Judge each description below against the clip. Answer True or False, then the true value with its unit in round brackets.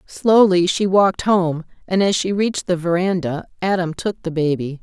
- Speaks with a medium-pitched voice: True (180 Hz)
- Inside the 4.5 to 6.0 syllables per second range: True (4.9 syllables/s)